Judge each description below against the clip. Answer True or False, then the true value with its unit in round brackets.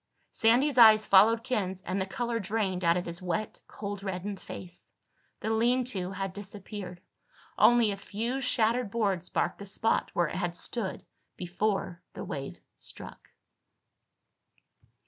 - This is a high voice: True (200 Hz)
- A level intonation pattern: False (3.6 semitones)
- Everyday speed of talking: True (145 wpm)